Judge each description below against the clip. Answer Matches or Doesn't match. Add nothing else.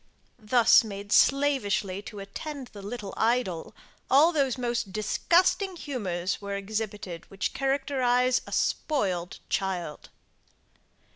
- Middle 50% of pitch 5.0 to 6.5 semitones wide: Matches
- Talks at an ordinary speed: Doesn't match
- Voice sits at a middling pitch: Doesn't match